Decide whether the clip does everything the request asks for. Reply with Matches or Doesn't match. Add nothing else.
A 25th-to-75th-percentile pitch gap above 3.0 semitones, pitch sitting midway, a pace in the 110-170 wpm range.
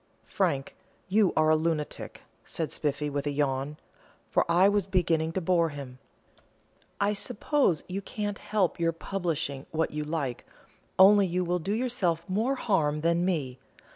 Matches